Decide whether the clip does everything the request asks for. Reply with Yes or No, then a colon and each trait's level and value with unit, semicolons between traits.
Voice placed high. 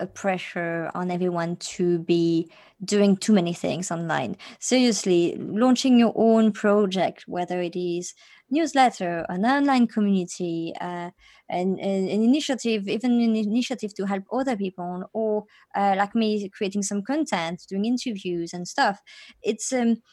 Yes: high, 200 Hz